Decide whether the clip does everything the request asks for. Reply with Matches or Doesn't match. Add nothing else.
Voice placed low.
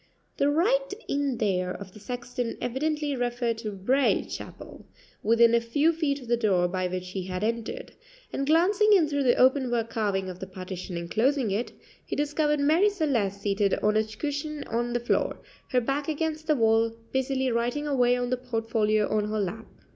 Doesn't match